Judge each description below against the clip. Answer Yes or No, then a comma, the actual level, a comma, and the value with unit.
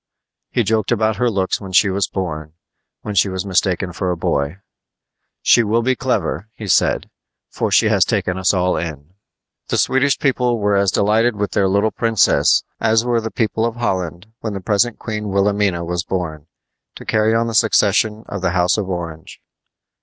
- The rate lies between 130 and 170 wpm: No, average, 185 wpm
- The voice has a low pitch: Yes, low, 100 Hz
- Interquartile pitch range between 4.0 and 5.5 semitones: No, average, 3.5 semitones